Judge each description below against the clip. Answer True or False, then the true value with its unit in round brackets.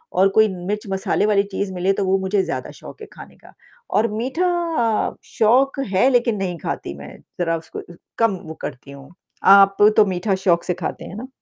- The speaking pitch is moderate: False (195 Hz)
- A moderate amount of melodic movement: True (3.2 semitones)